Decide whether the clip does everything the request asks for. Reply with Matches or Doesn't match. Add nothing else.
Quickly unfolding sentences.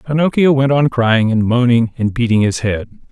Doesn't match